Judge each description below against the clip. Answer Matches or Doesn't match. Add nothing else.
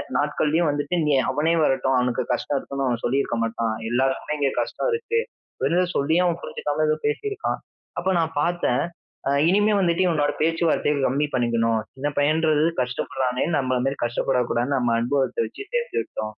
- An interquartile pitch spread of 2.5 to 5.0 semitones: Matches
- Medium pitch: Matches